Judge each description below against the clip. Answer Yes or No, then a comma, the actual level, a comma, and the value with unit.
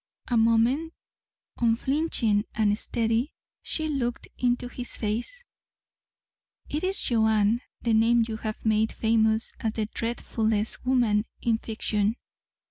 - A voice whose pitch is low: No, high, 225 Hz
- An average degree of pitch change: No, narrow, 1.9 semitones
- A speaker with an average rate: No, slow, 120 wpm